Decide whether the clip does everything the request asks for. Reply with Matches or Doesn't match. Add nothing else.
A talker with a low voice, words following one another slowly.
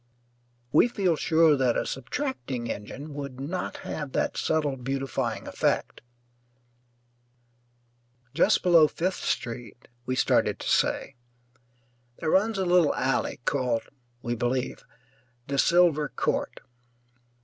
Doesn't match